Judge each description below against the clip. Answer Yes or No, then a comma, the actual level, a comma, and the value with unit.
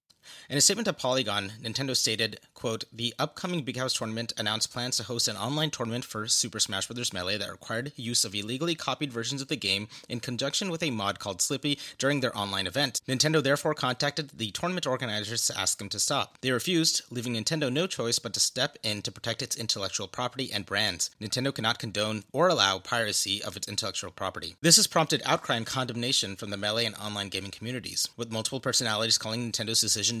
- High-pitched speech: No, low, 120 Hz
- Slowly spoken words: No, fast, 205 wpm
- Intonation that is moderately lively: Yes, average, 4.3 semitones